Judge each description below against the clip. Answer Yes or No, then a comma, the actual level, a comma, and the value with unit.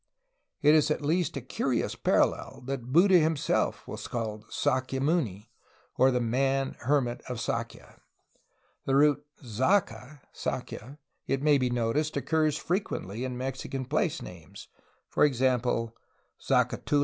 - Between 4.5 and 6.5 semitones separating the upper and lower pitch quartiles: No, average, 3.6 semitones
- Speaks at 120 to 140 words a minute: Yes, slow, 135 wpm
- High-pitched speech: No, low, 135 Hz